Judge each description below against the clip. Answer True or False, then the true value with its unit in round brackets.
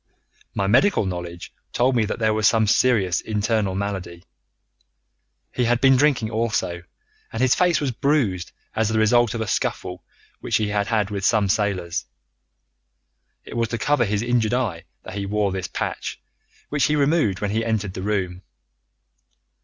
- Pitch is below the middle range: True (110 Hz)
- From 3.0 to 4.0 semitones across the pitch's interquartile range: True (3.5 semitones)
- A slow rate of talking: False (170 wpm)